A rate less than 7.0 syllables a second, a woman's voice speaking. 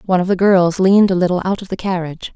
No: 7.2 syllables/s; female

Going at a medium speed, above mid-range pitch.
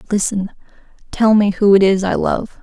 Yes: average, 185 wpm; high, 200 Hz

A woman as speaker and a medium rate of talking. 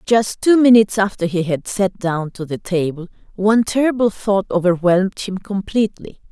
Yes: female; average, 160 wpm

